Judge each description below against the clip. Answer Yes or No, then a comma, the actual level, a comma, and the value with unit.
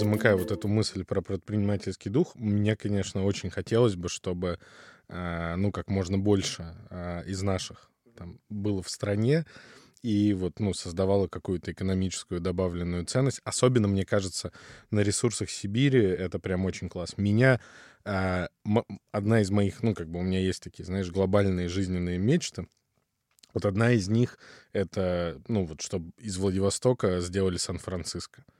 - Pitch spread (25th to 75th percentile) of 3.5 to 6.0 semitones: No, narrow, 2.6 semitones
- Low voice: Yes, low, 100 Hz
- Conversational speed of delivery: Yes, average, 145 wpm